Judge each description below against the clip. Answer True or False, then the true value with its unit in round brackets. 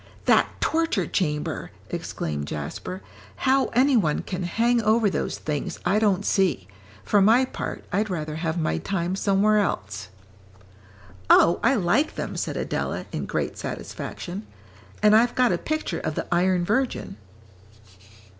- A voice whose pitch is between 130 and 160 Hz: False (195 Hz)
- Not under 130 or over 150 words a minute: True (145 wpm)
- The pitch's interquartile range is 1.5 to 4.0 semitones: False (5.4 semitones)